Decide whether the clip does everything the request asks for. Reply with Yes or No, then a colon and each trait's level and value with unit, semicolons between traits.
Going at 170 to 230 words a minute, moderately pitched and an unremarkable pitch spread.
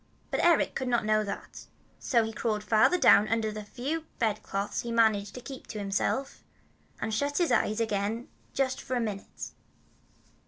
No: average, 180 wpm; high, 225 Hz; average, 3.4 semitones